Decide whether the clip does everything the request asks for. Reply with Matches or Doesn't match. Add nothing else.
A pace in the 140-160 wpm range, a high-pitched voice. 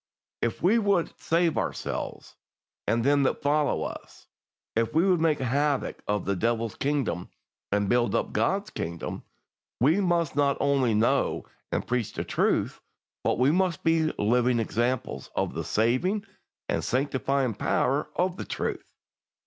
Doesn't match